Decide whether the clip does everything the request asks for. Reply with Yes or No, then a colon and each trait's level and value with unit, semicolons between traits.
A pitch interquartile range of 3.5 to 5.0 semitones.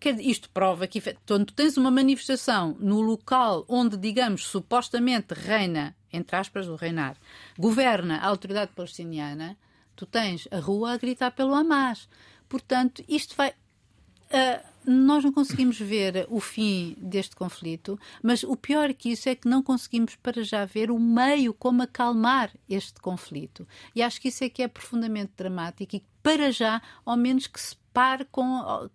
Yes: average, 4.7 semitones